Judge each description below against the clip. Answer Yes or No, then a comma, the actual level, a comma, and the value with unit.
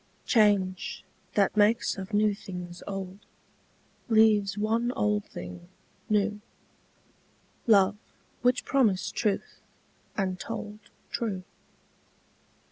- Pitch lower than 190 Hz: No, high, 205 Hz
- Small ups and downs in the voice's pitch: Yes, narrow, 2.1 semitones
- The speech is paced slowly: Yes, slow, 90 wpm